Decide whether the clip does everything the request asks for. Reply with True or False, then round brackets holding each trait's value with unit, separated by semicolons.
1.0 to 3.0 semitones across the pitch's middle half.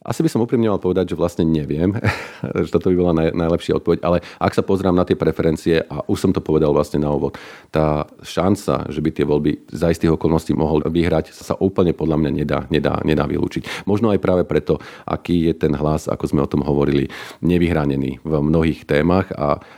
False (3.5 semitones)